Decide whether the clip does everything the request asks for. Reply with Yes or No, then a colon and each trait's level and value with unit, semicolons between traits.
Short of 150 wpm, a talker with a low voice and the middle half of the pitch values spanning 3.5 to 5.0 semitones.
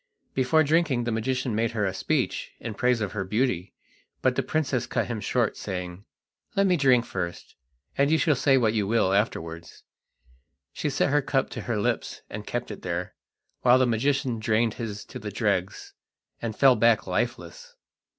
No: average, 180 wpm; low, 115 Hz; average, 4.2 semitones